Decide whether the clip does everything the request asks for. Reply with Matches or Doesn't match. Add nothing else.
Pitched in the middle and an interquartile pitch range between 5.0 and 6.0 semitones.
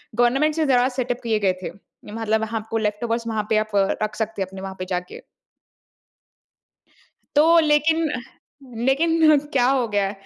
Doesn't match